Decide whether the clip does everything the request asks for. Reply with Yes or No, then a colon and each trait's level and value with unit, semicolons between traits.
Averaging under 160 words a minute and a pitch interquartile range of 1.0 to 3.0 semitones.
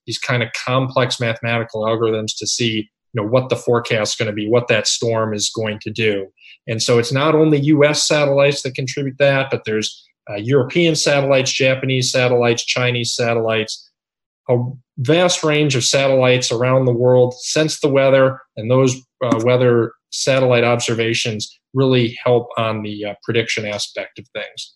No: average, 165 wpm; average, 2.7 semitones